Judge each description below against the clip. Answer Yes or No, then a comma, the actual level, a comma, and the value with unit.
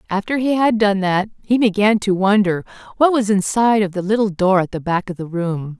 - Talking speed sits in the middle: No, fast, 230 wpm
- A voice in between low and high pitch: No, high, 200 Hz